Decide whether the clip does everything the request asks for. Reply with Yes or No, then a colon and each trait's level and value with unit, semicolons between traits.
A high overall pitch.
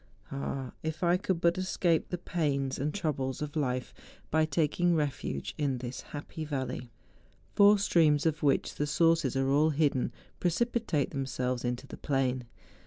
No: medium, 150 Hz